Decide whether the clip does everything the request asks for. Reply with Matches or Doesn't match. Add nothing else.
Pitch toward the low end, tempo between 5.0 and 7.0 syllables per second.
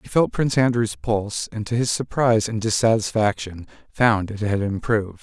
Matches